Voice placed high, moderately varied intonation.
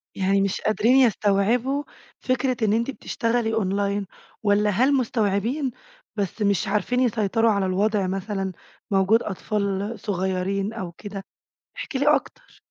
Yes: high, 210 Hz; average, 3.1 semitones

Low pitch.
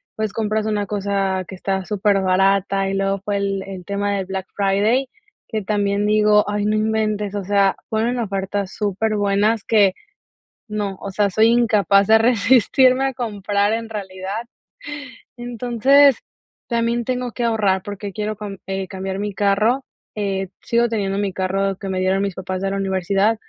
No: high, 205 Hz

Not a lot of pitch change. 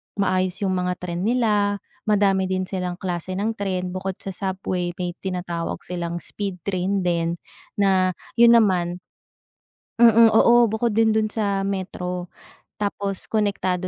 Yes: narrow, 2.1 semitones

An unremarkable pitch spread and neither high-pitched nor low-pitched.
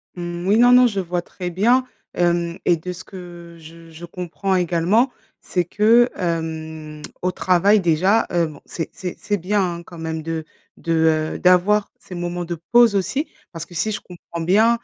Yes: average, 3.2 semitones; medium, 175 Hz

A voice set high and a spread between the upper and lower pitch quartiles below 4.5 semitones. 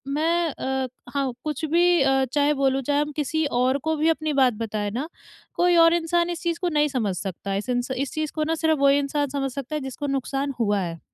Yes: very high, 285 Hz; average, 3.3 semitones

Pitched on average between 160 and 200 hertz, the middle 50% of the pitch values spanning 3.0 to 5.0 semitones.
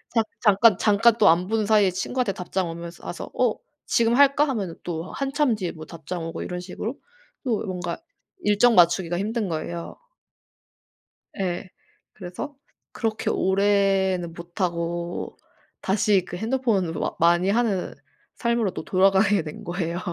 Yes: high, 190 Hz; average, 4.1 semitones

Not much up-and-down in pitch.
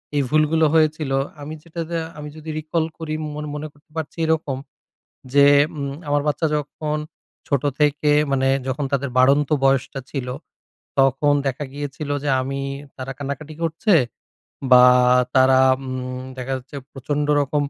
Yes: narrow, 2.2 semitones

